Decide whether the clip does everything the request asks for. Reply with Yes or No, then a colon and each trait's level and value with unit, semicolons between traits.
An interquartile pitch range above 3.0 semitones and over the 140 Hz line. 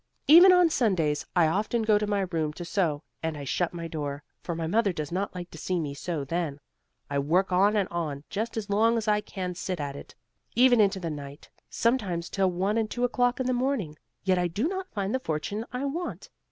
Yes: wide, 5.6 semitones; high, 190 Hz